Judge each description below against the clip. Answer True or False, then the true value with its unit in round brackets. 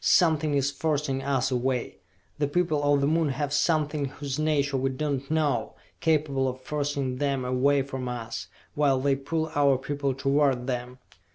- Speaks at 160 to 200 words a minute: True (170 wpm)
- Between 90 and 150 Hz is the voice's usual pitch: True (140 Hz)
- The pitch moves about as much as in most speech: False (2.0 semitones)